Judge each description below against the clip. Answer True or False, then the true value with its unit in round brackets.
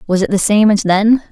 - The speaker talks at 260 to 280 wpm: True (275 wpm)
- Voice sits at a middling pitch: False (205 Hz)